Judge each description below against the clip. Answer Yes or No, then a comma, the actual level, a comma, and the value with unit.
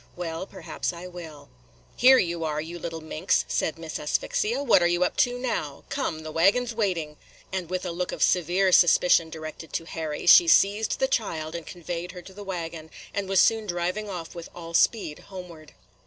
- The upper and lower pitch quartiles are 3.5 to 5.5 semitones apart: No, average, 3.1 semitones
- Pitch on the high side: No, medium, 175 Hz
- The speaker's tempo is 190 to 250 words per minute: Yes, average, 200 wpm